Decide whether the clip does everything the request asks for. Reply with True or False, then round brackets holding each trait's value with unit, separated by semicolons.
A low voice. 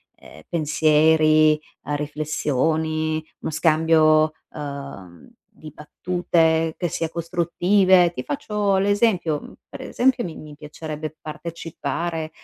False (155 Hz)